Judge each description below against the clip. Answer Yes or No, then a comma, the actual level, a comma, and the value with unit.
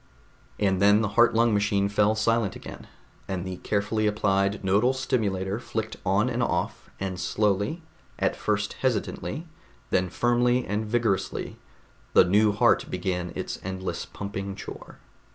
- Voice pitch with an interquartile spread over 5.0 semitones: No, average, 2.7 semitones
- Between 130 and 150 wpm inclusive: Yes, average, 140 wpm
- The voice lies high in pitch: No, low, 105 Hz